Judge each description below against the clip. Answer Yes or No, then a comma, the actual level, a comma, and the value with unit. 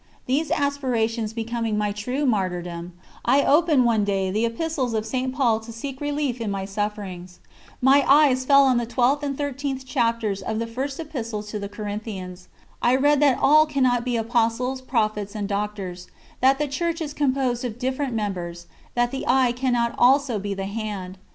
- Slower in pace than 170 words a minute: No, average, 175 wpm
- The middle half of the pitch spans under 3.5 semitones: No, average, 4.4 semitones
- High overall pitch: Yes, high, 240 Hz